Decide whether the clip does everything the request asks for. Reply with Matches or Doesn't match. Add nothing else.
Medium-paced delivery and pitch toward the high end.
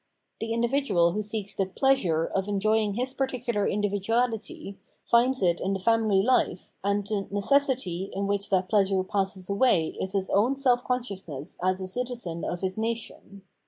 Matches